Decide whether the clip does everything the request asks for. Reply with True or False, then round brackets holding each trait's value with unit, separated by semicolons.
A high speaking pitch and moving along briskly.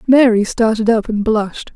False (225 Hz; 170 wpm)